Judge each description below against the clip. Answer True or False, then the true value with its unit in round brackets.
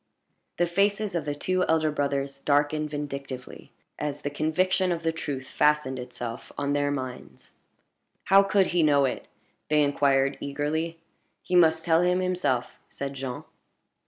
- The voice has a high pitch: False (150 Hz)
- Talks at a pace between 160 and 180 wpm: False (150 wpm)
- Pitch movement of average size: True (3.5 semitones)